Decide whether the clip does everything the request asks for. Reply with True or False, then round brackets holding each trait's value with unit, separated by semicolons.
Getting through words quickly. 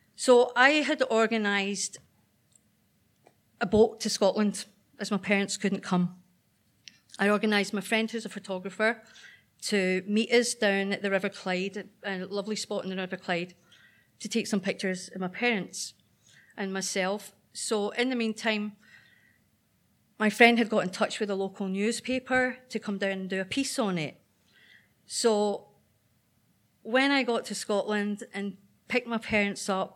False (155 wpm)